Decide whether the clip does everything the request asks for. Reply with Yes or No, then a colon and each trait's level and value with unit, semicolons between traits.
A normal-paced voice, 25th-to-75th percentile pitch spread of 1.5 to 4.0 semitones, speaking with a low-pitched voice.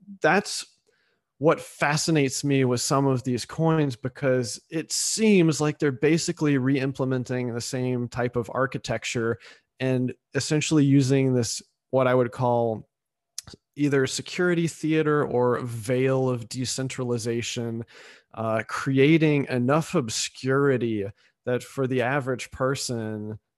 No: slow, 115 wpm; average, 3.1 semitones; low, 130 Hz